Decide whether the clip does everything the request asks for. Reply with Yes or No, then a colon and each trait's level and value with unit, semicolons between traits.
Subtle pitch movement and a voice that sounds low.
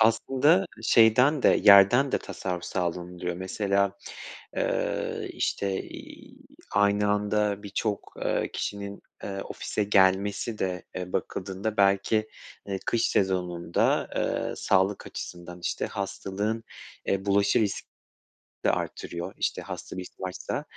Yes: narrow, 2.0 semitones; low, 100 Hz